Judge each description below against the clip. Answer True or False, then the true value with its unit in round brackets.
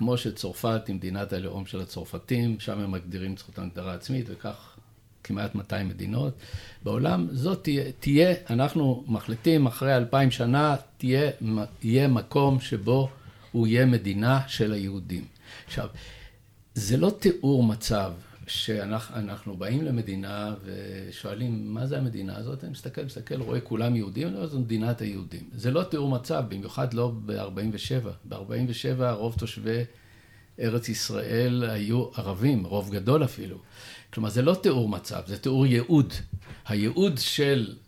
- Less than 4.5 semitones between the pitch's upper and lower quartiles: True (4.0 semitones)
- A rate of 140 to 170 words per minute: True (145 wpm)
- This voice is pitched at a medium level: False (115 Hz)